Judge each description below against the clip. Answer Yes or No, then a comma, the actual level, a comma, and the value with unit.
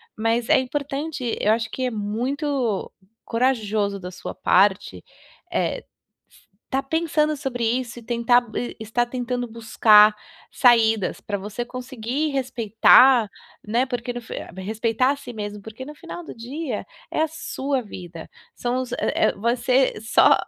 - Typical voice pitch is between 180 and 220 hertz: No, high, 240 Hz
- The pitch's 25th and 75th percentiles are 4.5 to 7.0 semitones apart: No, average, 3.2 semitones